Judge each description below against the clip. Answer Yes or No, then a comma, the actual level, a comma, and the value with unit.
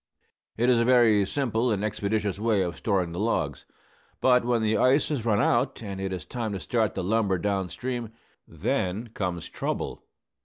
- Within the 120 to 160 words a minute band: No, average, 185 wpm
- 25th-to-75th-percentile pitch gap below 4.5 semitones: Yes, average, 3.5 semitones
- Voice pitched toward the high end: No, low, 110 Hz